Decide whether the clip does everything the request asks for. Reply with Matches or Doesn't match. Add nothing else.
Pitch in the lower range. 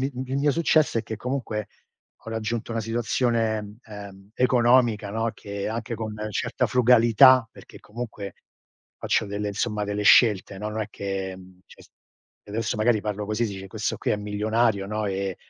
Matches